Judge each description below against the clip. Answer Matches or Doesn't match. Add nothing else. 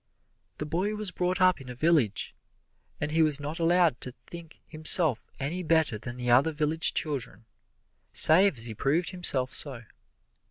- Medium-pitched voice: Matches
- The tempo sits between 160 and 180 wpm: Matches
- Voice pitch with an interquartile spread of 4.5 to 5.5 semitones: Matches